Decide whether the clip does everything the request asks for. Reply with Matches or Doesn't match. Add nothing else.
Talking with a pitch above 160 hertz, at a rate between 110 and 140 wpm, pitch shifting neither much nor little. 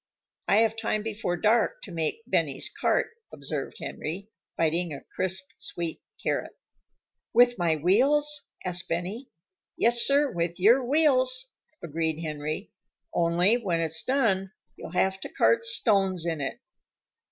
Doesn't match